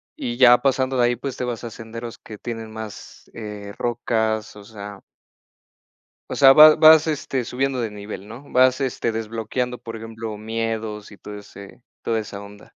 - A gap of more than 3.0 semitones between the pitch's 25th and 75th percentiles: No, average, 2.7 semitones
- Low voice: Yes, low, 115 Hz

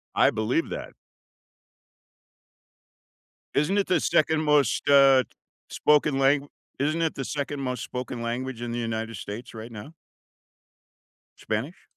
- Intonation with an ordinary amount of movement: Yes, average, 4.0 semitones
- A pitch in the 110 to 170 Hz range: Yes, low, 135 Hz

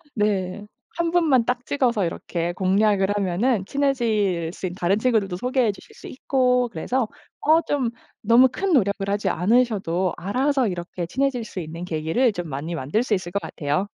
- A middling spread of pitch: No, wide, 5.8 semitones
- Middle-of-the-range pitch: No, high, 210 Hz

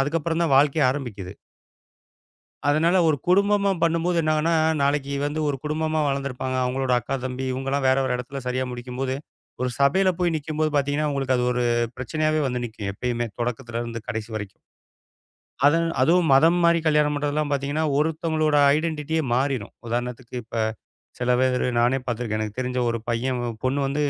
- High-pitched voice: No, medium, 140 Hz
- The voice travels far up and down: No, average, 3.8 semitones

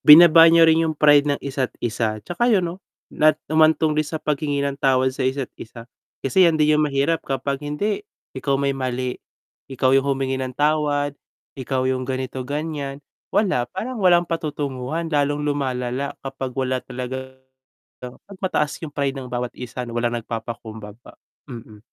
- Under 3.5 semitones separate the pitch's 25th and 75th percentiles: Yes, average, 3.0 semitones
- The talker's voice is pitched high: No, medium, 140 Hz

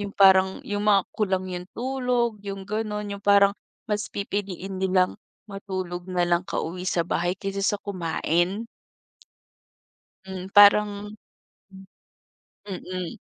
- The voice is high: Yes, high, 195 Hz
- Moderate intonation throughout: No, narrow, 2.0 semitones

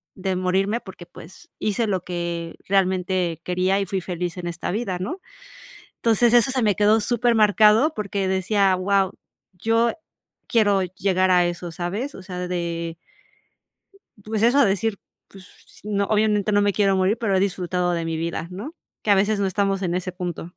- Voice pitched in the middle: No, high, 195 Hz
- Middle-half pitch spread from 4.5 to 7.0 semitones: No, average, 2.8 semitones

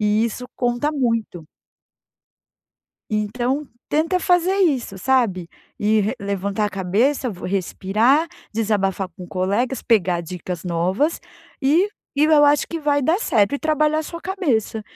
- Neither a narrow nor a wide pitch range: No, wide, 6.9 semitones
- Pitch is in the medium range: No, high, 230 Hz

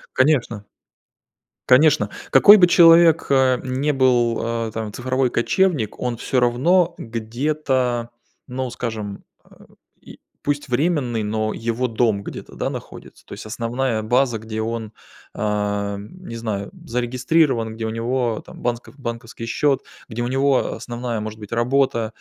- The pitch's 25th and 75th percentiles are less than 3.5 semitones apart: Yes, average, 3.1 semitones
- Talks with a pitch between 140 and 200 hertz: No, low, 120 Hz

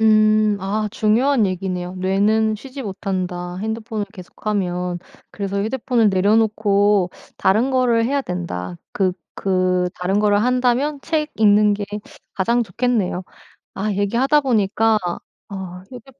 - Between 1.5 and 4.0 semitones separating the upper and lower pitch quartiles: Yes, average, 3.4 semitones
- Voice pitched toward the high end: Yes, high, 210 Hz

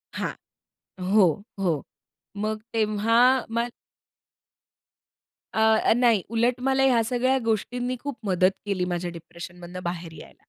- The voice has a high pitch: Yes, high, 220 Hz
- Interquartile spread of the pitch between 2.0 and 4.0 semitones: No, average, 5.1 semitones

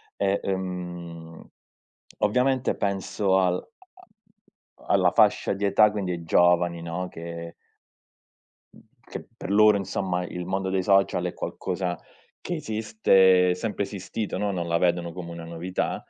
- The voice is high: No, very low, 95 Hz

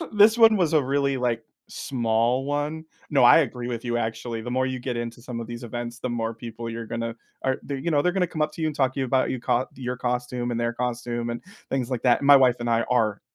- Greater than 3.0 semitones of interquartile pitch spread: No, narrow, 2.6 semitones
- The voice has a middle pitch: No, low, 125 Hz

